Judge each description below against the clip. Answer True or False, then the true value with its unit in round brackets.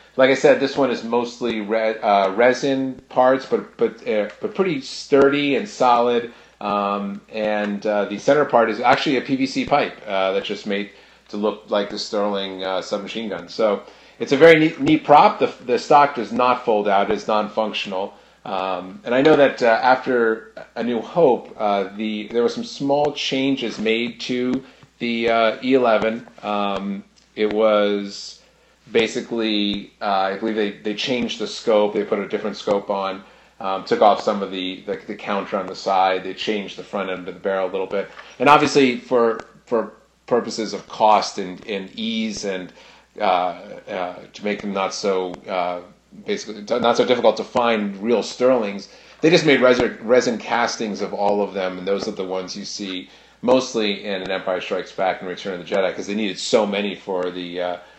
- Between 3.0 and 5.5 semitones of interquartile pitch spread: True (4.1 semitones)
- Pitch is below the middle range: True (105 Hz)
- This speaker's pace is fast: False (190 wpm)